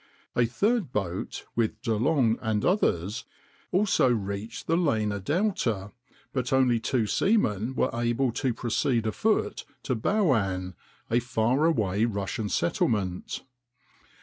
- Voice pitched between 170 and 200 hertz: No, low, 115 Hz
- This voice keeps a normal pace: No, slow, 120 wpm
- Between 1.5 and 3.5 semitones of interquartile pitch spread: No, average, 4.2 semitones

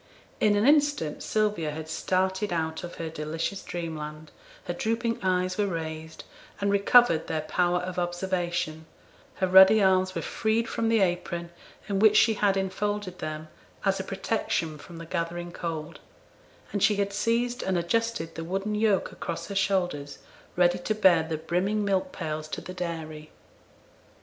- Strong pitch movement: No, average, 3.8 semitones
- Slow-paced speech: No, average, 160 wpm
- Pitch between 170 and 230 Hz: Yes, medium, 185 Hz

